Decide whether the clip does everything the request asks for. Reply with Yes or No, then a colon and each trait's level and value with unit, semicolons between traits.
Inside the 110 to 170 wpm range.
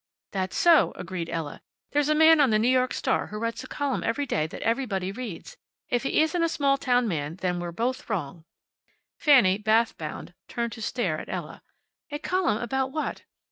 No: average, 195 wpm